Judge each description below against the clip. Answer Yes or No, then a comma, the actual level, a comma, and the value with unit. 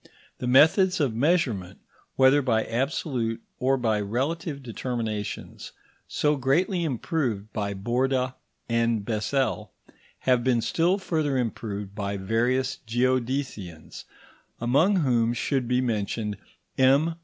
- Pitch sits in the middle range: No, low, 125 Hz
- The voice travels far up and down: No, average, 3.7 semitones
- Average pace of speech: No, slow, 110 wpm